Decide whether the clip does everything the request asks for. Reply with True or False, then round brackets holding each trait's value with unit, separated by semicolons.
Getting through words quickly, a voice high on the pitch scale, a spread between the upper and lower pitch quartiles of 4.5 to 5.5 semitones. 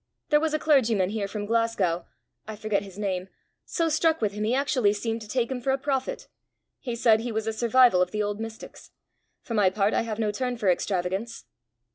False (215 wpm; 220 Hz; 3.4 semitones)